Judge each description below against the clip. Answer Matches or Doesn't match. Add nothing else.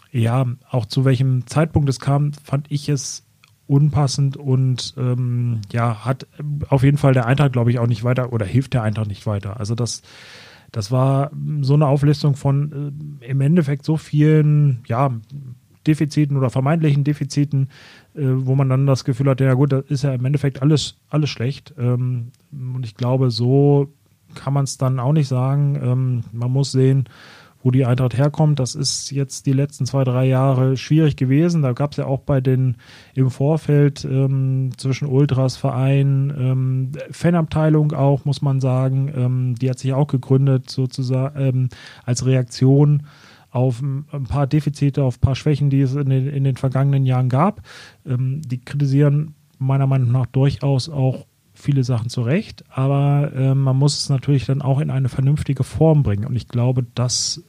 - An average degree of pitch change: Doesn't match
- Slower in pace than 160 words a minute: Doesn't match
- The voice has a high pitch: Doesn't match